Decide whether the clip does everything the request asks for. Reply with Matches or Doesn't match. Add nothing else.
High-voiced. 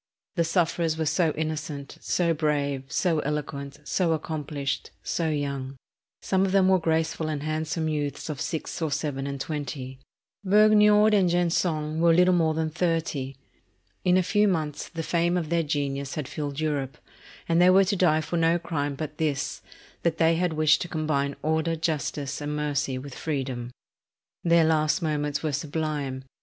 Doesn't match